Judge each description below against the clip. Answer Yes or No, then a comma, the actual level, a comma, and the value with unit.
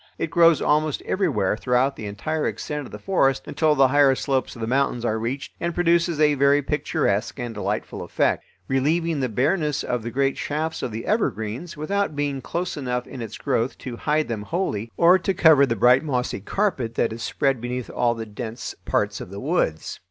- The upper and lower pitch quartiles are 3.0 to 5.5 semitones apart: Yes, average, 4.8 semitones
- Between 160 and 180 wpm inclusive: No, average, 200 wpm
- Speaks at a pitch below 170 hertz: Yes, low, 135 Hz